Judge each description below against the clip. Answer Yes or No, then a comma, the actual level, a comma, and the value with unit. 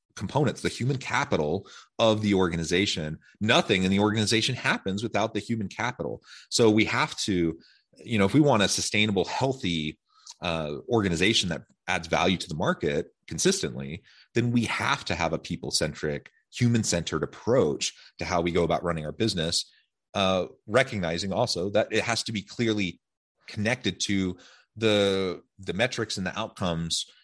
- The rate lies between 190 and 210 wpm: No, average, 155 wpm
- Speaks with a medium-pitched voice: No, low, 100 Hz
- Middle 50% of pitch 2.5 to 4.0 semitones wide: No, average, 4.4 semitones